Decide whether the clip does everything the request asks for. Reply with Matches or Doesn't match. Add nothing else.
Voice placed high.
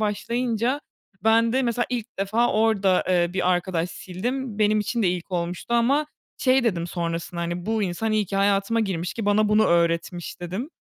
Matches